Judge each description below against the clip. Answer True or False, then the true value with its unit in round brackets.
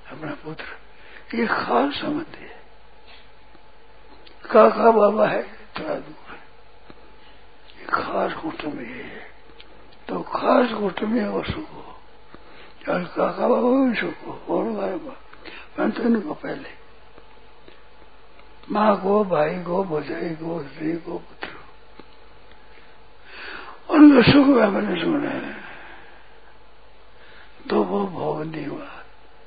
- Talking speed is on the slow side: True (105 wpm)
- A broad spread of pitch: True (8.3 semitones)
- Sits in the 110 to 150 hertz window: False (220 Hz)